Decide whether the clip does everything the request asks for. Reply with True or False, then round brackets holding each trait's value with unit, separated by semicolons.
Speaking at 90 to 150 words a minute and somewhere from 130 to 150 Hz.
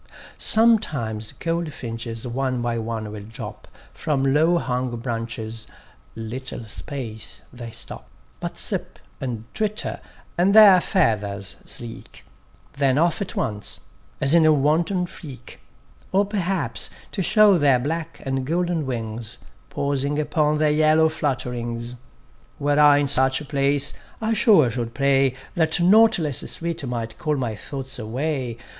True (135 wpm; 140 Hz)